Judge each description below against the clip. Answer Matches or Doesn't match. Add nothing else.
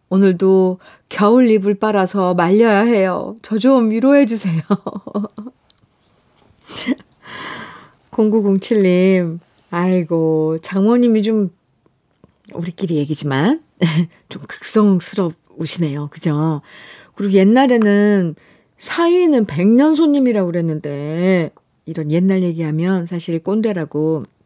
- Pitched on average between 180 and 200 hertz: Matches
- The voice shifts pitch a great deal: Doesn't match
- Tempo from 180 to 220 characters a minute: Matches